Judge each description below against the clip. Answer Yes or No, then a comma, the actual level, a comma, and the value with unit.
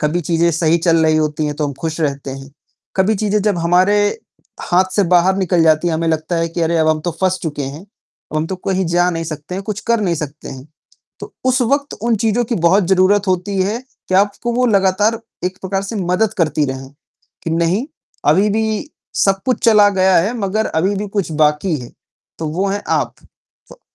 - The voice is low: No, medium, 185 Hz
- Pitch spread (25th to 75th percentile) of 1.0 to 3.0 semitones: No, average, 4.0 semitones